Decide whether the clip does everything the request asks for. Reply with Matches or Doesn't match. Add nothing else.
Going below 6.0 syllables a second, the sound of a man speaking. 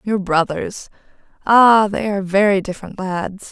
Doesn't match